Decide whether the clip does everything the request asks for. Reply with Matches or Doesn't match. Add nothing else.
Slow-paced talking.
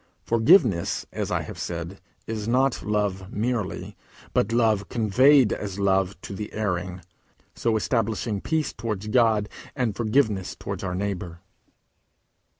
Matches